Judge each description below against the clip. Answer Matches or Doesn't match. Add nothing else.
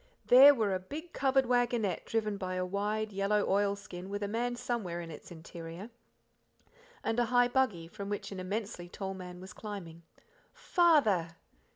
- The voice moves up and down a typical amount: Matches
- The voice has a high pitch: Matches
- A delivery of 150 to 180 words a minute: Matches